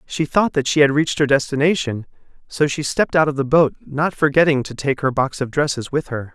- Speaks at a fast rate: Yes, fast, 235 wpm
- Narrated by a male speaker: Yes, male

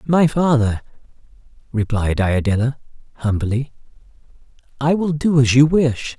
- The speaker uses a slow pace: Yes, slow, 105 wpm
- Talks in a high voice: No, low, 130 Hz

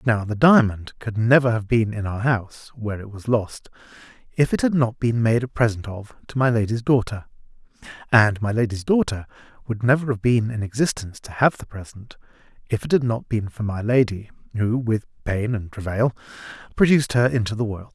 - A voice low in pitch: Yes, low, 115 Hz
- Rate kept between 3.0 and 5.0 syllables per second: No, 5.4 syllables/s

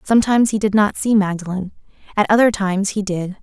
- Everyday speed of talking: Yes, average, 195 wpm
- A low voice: No, high, 205 Hz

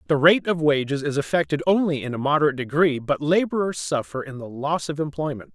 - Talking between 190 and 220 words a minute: Yes, fast, 205 wpm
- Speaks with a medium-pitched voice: Yes, medium, 145 Hz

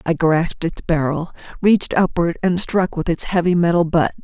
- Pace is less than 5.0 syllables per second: No, 5.1 syllables/s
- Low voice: No, medium, 170 Hz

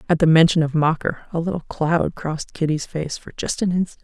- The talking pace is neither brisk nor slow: No, fast, 225 wpm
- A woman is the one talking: Yes, female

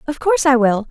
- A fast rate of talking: Yes, fast, 265 wpm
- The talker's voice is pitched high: Yes, very high, 250 Hz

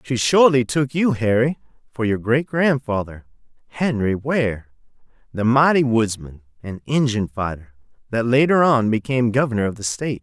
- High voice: No, low, 120 Hz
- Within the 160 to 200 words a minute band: No, average, 145 wpm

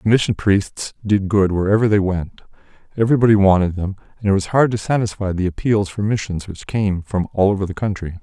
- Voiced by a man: Yes, male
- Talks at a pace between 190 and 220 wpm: Yes, fast, 205 wpm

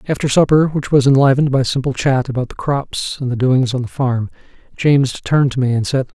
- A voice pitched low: Yes, low, 130 Hz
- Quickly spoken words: Yes, fast, 225 wpm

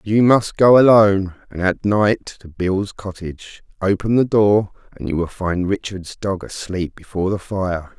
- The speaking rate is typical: Yes, average, 175 wpm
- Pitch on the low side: Yes, low, 100 Hz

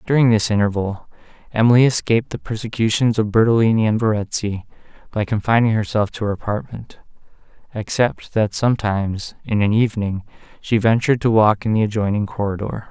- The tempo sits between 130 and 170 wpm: Yes, average, 145 wpm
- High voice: No, low, 110 Hz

